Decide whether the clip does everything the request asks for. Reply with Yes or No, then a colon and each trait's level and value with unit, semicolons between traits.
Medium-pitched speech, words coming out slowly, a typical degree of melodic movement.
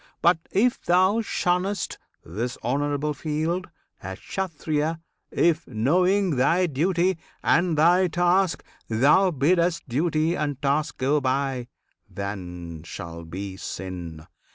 No: medium, 150 Hz; slow, 110 wpm; wide, 6.5 semitones